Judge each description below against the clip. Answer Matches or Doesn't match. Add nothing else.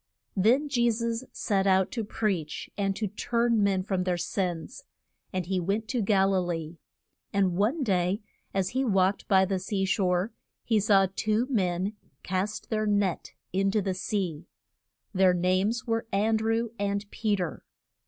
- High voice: Matches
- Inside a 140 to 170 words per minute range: Matches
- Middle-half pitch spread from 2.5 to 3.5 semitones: Matches